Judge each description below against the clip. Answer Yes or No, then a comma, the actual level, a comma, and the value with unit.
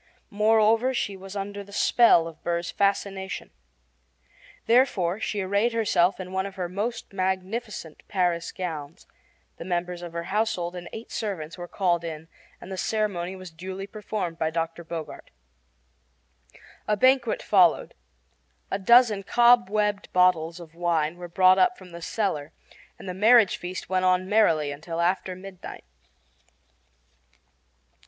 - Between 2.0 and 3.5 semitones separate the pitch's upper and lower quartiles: Yes, average, 3.2 semitones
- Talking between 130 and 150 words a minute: Yes, average, 140 wpm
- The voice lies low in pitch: No, medium, 185 Hz